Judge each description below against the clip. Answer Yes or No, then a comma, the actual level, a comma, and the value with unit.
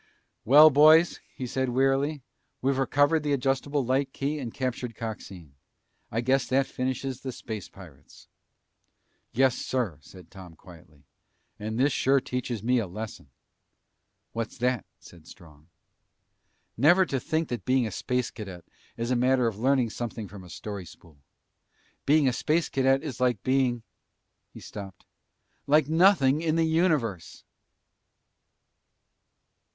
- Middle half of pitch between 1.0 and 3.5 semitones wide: No, average, 4.3 semitones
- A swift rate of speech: No, average, 140 wpm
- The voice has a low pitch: Yes, low, 125 Hz